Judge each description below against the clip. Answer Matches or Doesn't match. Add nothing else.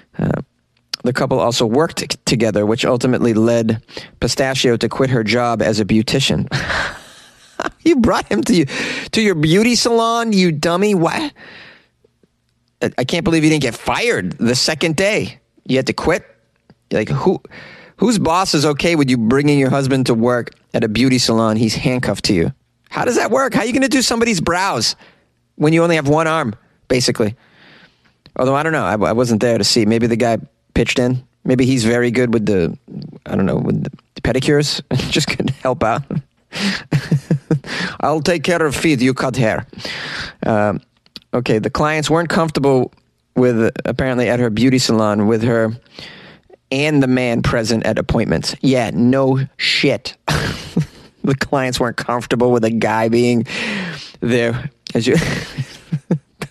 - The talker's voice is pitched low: Matches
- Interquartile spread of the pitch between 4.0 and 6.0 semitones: Matches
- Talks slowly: Doesn't match